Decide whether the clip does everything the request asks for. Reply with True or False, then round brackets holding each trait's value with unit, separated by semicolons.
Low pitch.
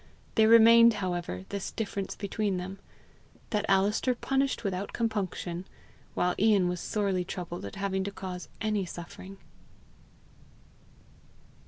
False (195 Hz)